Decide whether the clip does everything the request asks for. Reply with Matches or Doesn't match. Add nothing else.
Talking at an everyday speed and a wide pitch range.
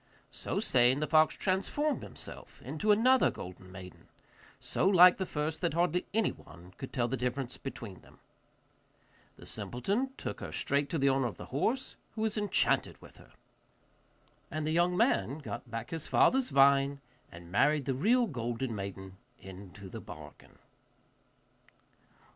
Matches